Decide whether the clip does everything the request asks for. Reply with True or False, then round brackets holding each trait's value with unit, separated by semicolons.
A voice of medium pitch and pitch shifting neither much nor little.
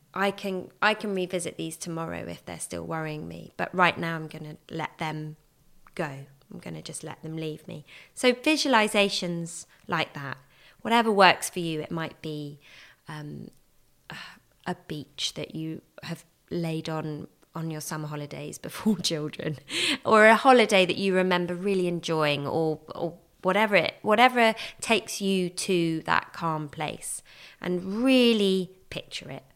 True (170 Hz; 4.1 semitones)